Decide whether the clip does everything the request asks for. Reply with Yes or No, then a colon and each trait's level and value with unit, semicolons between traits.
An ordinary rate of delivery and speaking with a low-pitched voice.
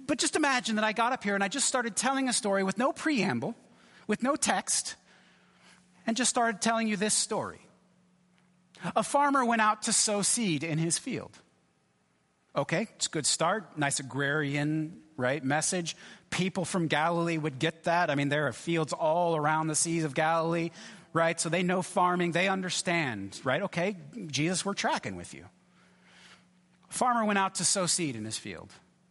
No: average, 180 wpm; medium, 180 Hz